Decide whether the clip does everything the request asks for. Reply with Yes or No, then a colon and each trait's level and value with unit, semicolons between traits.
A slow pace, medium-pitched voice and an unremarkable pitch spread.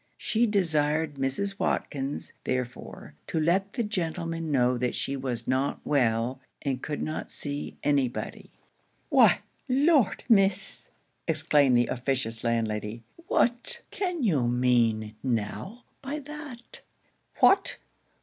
No: slow, 120 wpm; medium, 145 Hz; wide, 8.2 semitones